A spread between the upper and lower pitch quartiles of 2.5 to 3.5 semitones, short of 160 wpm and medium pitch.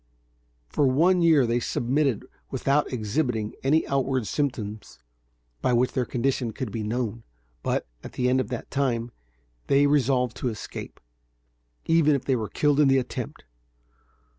No: average, 3.2 semitones; average, 150 wpm; low, 130 Hz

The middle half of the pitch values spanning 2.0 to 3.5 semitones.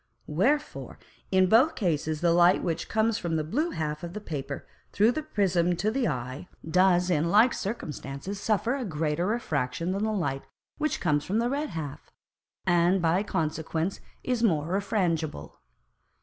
No: average, 5.3 semitones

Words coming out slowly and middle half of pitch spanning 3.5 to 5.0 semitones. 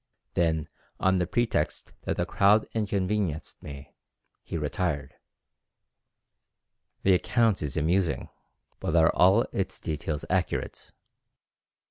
Yes: slow, 105 wpm; average, 4.0 semitones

